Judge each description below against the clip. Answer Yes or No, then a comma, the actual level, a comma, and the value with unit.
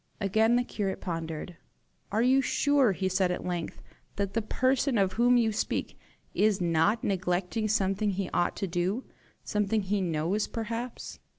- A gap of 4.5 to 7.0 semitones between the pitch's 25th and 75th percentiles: No, average, 3.8 semitones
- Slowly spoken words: No, average, 160 wpm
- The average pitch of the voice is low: No, high, 200 Hz